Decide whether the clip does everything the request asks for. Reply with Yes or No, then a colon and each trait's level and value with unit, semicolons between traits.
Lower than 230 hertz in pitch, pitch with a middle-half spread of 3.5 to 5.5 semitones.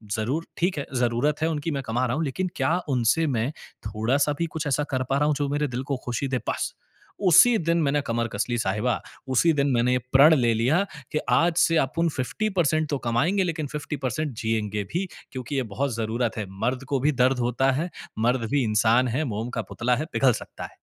Yes: low, 135 Hz; average, 4.4 semitones